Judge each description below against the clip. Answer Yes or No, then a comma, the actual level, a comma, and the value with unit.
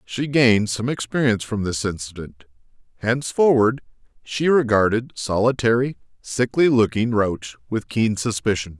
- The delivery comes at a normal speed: No, slow, 115 wpm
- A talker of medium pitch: No, low, 115 Hz